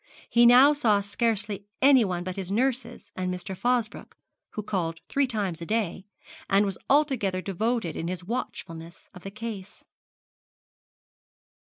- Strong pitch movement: No, average, 4.5 semitones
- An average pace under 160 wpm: Yes, average, 140 wpm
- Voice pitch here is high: Yes, high, 205 Hz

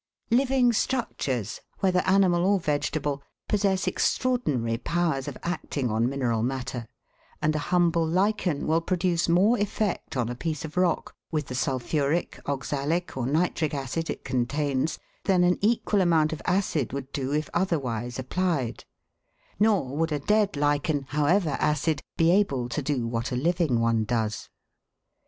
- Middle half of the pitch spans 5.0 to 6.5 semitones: Yes, wide, 5.4 semitones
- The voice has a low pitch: No, medium, 155 Hz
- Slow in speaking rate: No, average, 150 wpm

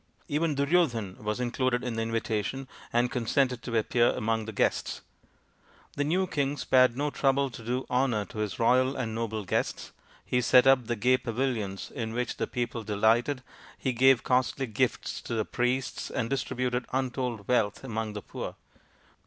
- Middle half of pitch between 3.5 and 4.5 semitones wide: No, average, 2.7 semitones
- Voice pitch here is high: No, low, 125 Hz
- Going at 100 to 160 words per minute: No, average, 170 wpm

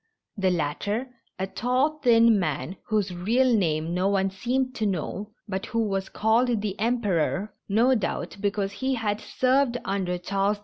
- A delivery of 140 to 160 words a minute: No, average, 170 wpm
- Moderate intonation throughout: Yes, average, 3.8 semitones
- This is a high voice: Yes, high, 205 Hz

